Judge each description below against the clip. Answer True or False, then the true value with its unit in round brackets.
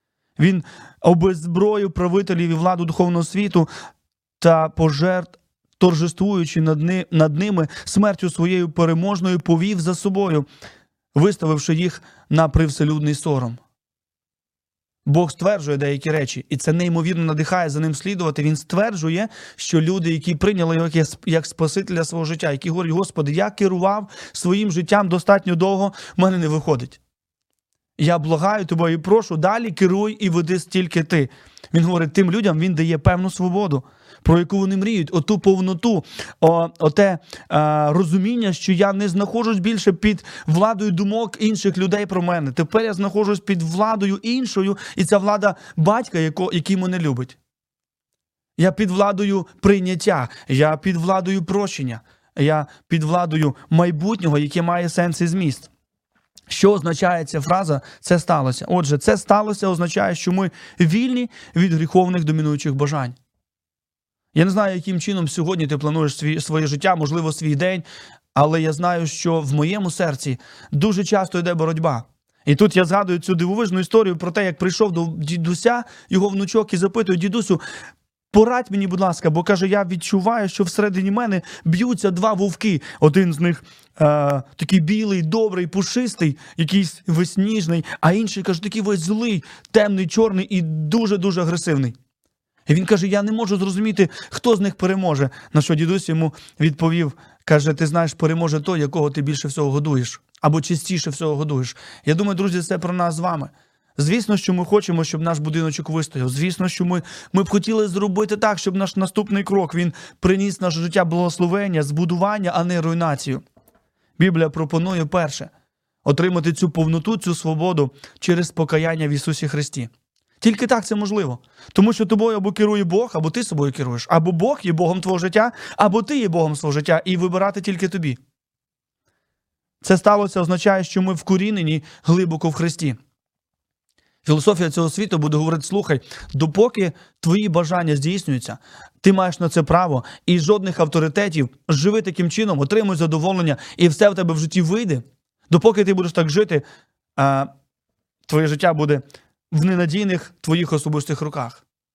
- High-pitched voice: False (175 Hz)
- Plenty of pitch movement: False (3.8 semitones)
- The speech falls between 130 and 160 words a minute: True (150 wpm)